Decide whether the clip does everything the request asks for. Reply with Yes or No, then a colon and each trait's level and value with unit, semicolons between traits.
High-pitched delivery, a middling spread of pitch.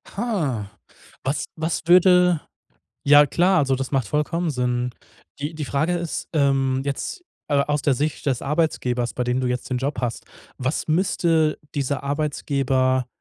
No: medium, 140 Hz; average, 3.6 semitones